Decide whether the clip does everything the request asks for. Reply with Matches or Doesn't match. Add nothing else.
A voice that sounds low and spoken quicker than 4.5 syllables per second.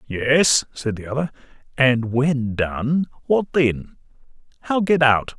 Doesn't match